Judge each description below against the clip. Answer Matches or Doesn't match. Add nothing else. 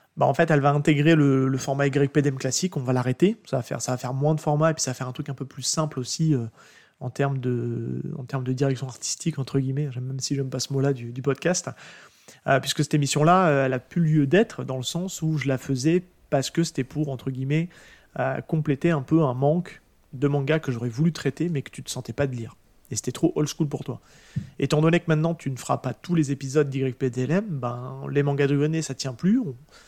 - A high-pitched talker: Doesn't match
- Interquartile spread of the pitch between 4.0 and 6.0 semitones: Doesn't match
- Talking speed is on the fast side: Matches